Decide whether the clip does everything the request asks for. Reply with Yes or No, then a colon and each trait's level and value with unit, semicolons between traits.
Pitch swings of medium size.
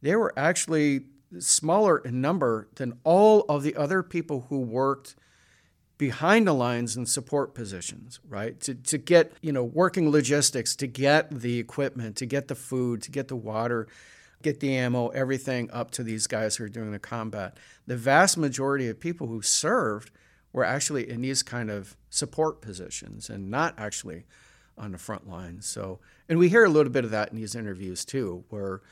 Yes: average, 4.9 semitones